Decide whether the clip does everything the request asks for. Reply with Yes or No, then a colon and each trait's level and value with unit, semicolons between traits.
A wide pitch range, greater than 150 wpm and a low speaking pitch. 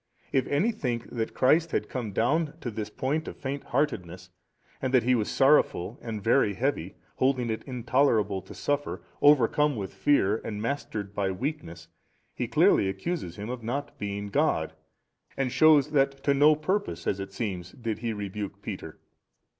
Yes: wide, 5.7 semitones; average, 170 wpm; low, 120 Hz